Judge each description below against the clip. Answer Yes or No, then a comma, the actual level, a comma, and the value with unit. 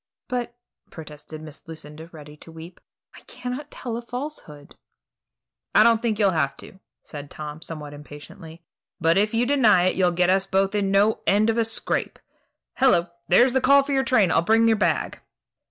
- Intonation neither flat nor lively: No, wide, 6.3 semitones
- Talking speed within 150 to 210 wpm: Yes, average, 185 wpm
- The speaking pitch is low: No, high, 190 Hz